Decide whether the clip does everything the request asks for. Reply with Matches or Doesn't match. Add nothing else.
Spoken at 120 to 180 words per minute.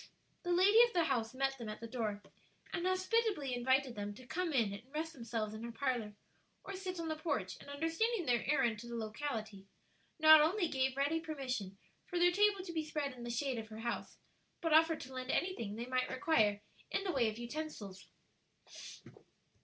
Doesn't match